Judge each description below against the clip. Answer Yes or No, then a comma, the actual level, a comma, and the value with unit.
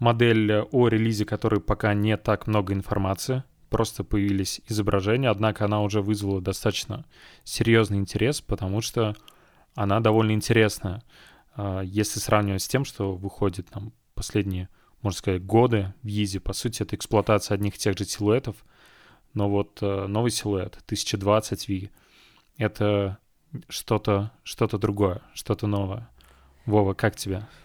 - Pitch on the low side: Yes, low, 105 Hz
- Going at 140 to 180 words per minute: No, average, 130 wpm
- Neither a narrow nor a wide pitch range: No, narrow, 1.7 semitones